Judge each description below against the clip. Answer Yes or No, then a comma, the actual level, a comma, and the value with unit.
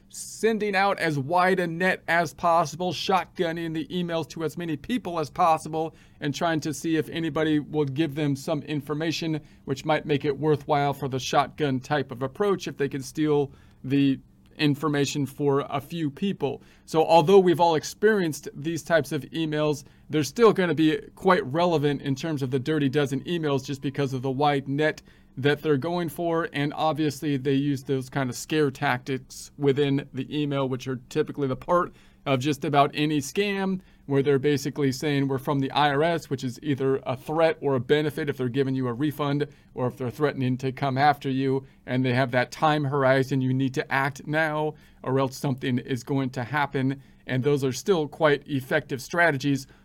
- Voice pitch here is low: No, medium, 145 Hz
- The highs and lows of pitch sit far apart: No, average, 2.7 semitones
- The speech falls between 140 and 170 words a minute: No, average, 190 wpm